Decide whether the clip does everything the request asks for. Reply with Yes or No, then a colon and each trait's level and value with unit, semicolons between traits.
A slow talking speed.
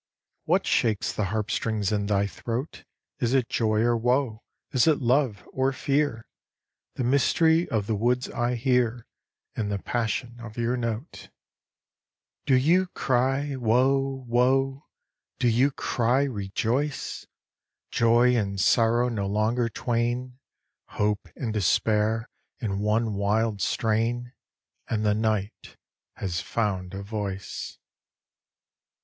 Yes: slow, 125 wpm